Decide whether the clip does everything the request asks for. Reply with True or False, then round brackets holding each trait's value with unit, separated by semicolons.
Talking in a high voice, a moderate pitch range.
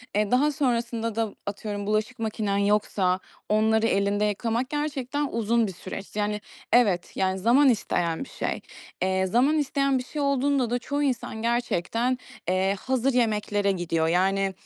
True (220 Hz; 4.1 semitones)